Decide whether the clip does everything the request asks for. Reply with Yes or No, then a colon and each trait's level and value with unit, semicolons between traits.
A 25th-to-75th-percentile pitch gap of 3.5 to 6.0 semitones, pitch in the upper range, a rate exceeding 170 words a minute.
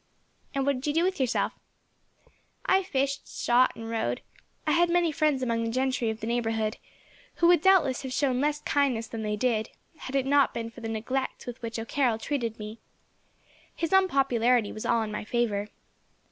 Yes: average, 3.9 semitones; very high, 250 Hz; average, 190 wpm